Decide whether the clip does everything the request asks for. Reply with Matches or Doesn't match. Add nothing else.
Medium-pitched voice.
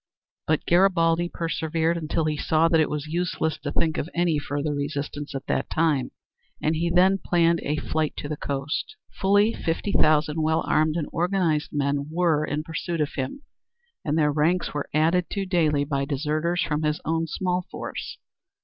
Matches